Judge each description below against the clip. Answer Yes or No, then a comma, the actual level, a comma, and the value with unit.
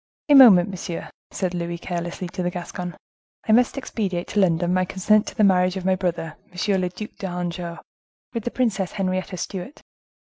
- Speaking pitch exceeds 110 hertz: Yes, medium, 185 Hz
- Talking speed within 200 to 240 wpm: No, average, 180 wpm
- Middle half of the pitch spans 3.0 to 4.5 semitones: No, narrow, 2.4 semitones